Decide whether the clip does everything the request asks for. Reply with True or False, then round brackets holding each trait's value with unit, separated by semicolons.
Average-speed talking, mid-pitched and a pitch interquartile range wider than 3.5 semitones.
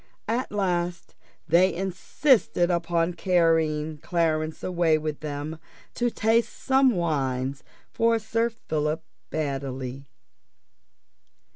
False (95 wpm; 170 Hz; 4.0 semitones)